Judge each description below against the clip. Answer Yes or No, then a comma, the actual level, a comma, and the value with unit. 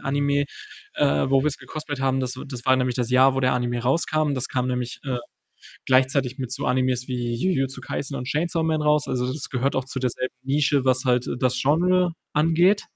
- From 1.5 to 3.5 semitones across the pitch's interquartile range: Yes, narrow, 2.5 semitones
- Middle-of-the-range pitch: No, low, 130 Hz